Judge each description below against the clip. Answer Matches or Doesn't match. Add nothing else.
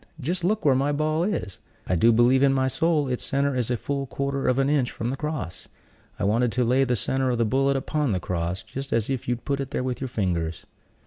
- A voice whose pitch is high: Doesn't match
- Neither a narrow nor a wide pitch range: Matches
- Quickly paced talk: Matches